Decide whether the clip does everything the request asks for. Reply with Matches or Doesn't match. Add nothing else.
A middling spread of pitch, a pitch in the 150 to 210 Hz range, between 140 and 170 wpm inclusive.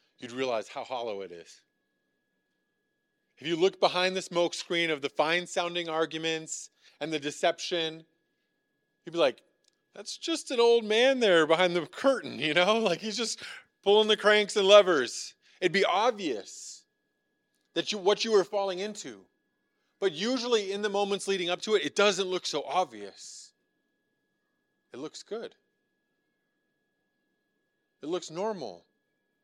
Matches